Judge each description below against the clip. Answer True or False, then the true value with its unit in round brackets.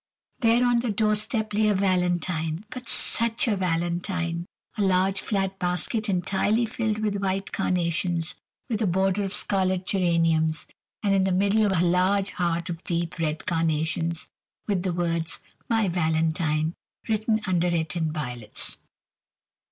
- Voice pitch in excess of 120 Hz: True (185 Hz)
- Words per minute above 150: False (145 wpm)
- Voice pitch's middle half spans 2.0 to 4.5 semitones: True (3.4 semitones)